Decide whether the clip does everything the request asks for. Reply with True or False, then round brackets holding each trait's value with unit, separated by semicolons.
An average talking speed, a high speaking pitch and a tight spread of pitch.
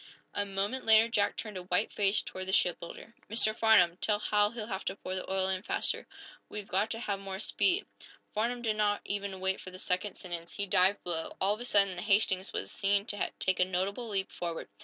False (220 wpm; 200 Hz; 2.2 semitones)